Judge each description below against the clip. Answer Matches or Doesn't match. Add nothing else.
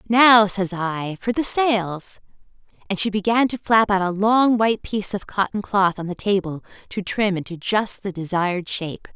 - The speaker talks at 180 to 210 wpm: Matches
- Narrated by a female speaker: Matches